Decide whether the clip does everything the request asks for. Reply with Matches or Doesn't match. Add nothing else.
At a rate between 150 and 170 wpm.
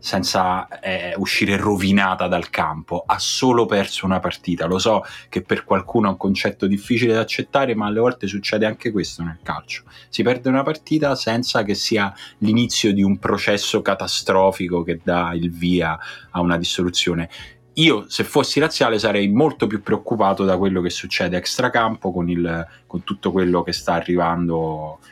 Matches